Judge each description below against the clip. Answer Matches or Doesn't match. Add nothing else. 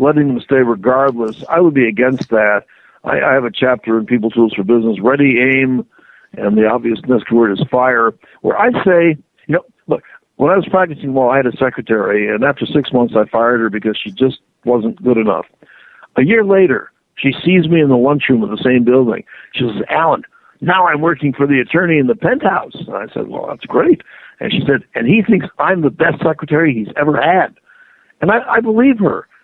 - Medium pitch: Doesn't match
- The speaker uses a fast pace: Matches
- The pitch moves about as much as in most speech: Doesn't match